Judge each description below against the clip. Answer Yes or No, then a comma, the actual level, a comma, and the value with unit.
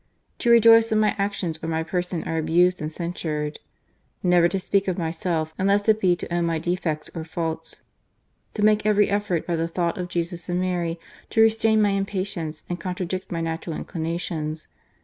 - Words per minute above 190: Yes, average, 200 wpm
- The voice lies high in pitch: No, medium, 175 Hz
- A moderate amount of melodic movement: Yes, average, 3.3 semitones